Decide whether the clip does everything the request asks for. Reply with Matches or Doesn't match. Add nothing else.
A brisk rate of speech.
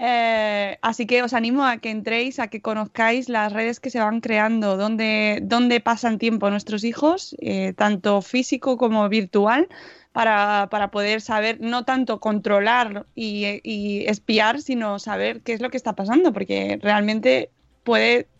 Doesn't match